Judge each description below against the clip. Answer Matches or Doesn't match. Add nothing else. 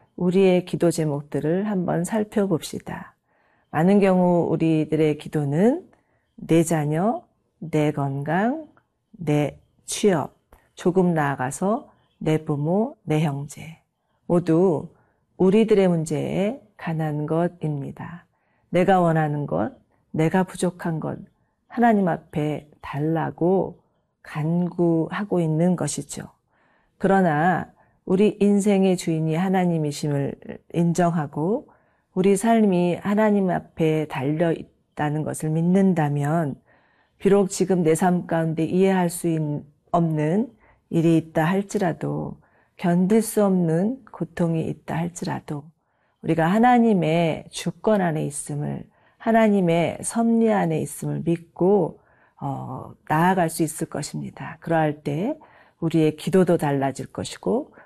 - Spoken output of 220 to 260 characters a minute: Matches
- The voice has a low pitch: Doesn't match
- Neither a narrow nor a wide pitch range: Matches